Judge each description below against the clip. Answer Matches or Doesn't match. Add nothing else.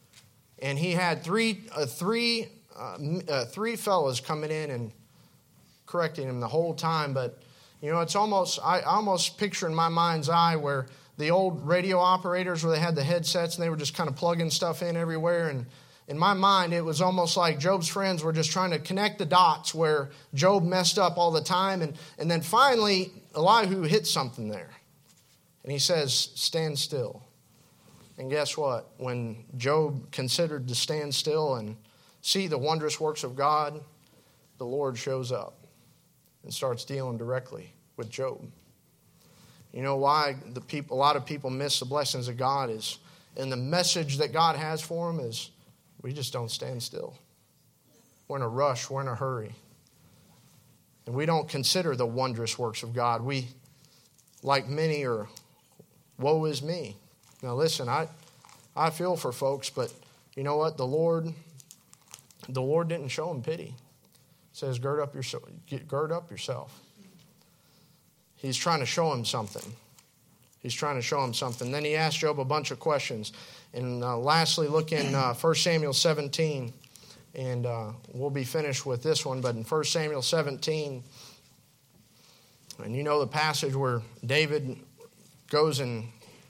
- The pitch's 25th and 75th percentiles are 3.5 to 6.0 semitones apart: Matches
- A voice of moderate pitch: Matches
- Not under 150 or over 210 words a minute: Matches